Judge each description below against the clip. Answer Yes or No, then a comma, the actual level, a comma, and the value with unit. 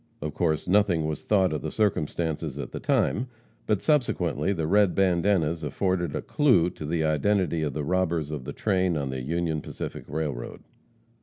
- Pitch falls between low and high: No, very low, 85 Hz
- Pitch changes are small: No, average, 3.7 semitones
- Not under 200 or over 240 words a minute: No, average, 175 wpm